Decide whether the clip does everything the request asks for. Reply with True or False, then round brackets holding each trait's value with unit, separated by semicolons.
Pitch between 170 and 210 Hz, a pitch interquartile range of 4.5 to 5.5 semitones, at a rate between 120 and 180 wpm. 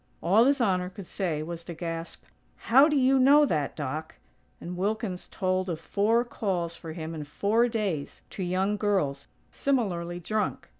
True (185 Hz; 4.8 semitones; 165 wpm)